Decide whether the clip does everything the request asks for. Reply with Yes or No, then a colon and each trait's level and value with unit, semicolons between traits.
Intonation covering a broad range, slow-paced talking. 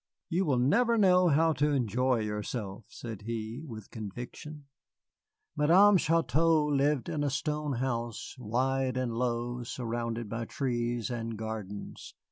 No: average, 4.5 semitones; slow, 130 wpm